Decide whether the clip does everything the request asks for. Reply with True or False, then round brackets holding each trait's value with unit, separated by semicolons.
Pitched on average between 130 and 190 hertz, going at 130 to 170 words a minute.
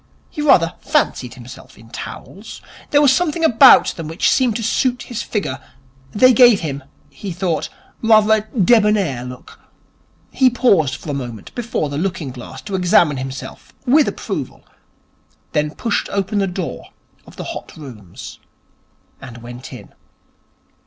True (185 Hz; 150 wpm)